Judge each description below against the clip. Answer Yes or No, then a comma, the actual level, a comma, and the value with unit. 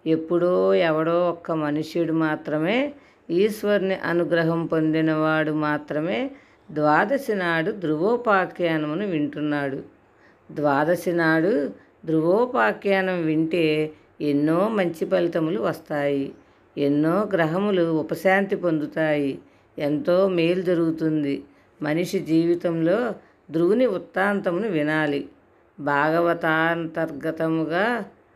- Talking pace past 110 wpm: No, slow, 70 wpm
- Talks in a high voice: No, medium, 165 Hz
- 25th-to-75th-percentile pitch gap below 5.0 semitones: Yes, average, 2.8 semitones